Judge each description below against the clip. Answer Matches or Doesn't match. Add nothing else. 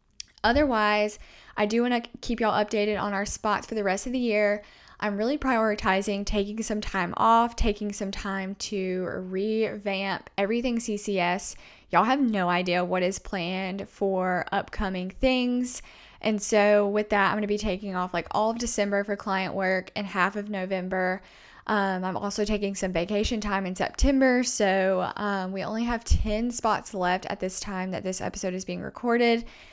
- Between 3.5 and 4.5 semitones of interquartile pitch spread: Doesn't match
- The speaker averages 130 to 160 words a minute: Doesn't match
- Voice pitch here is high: Matches